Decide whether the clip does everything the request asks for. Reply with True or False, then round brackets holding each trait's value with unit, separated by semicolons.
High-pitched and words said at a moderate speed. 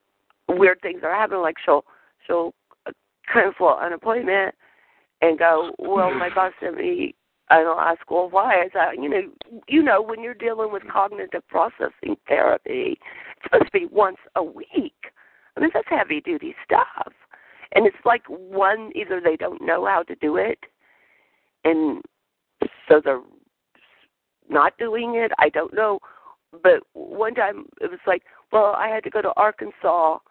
True (220 Hz; 165 wpm)